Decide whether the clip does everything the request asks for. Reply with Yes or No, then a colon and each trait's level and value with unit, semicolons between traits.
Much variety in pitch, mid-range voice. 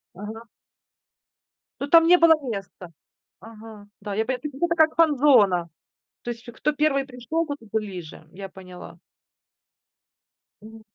No: wide, 6.5 semitones; high, 230 Hz